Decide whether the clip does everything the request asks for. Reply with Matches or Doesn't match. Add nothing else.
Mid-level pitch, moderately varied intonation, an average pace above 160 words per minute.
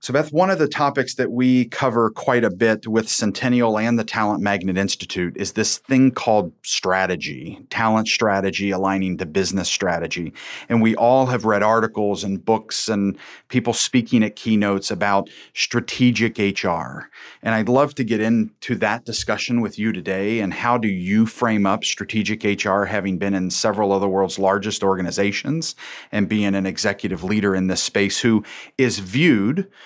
Doesn't match